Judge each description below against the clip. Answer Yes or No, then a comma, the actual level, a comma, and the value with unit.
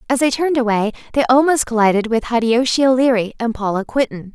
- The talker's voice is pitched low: No, high, 240 Hz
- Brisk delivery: No, average, 180 wpm